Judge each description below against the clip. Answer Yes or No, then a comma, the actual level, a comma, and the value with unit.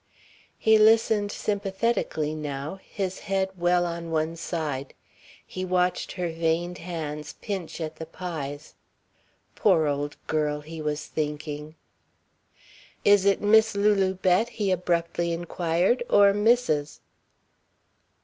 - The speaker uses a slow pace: Yes, slow, 115 wpm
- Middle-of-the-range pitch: Yes, medium, 175 Hz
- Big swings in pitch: No, average, 4.1 semitones